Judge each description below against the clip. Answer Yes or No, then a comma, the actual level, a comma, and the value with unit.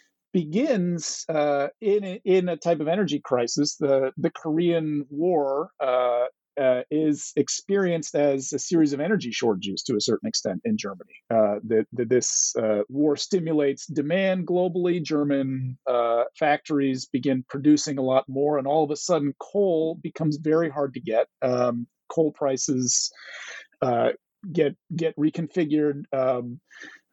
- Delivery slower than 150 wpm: Yes, average, 140 wpm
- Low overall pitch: No, medium, 150 Hz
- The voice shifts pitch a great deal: No, average, 4.1 semitones